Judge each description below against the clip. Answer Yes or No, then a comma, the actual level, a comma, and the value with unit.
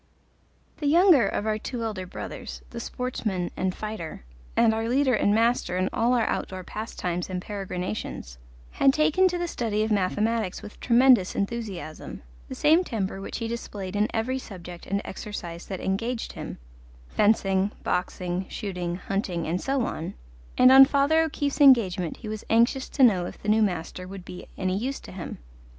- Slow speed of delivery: No, average, 170 wpm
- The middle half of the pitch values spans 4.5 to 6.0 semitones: Yes, average, 4.9 semitones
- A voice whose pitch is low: No, high, 215 Hz